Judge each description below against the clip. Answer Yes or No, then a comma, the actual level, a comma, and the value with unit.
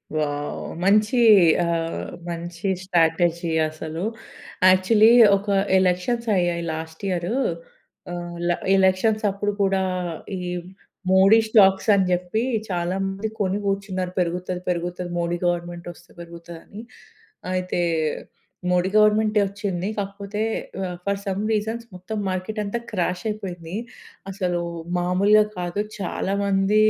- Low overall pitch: No, medium, 185 Hz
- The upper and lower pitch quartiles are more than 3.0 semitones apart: No, narrow, 2.6 semitones